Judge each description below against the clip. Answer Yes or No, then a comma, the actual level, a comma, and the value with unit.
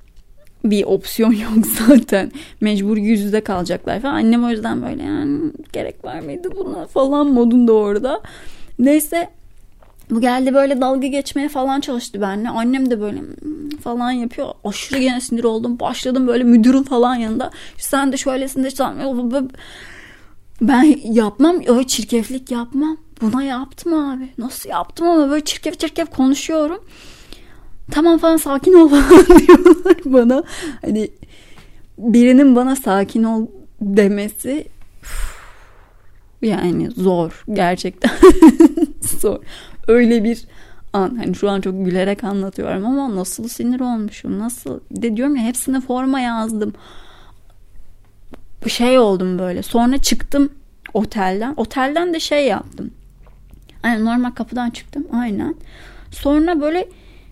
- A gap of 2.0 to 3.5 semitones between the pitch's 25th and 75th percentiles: No, average, 4.5 semitones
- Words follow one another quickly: No, average, 125 wpm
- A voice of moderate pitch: No, very high, 250 Hz